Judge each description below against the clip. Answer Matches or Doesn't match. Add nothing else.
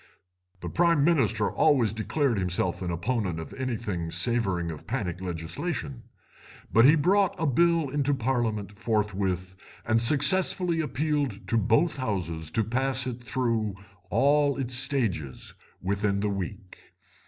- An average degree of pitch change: Doesn't match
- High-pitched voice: Doesn't match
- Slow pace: Matches